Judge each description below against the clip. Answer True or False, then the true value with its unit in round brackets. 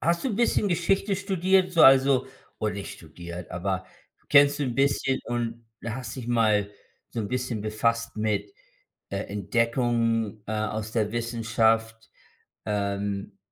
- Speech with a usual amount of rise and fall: True (4.1 semitones)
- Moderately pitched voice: False (115 Hz)